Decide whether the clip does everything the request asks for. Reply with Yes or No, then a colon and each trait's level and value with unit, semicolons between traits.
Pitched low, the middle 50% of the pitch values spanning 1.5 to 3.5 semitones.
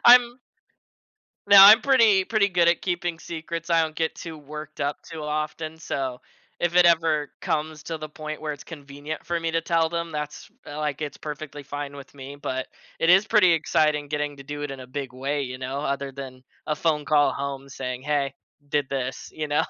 No: medium, 150 Hz; average, 2.8 semitones